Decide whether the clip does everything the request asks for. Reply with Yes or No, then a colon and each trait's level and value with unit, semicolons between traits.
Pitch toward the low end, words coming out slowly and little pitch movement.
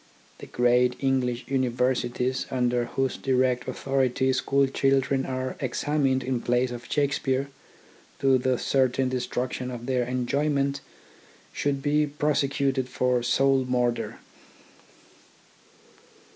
Yes: low, 130 Hz; slow, 115 wpm; narrow, 1.6 semitones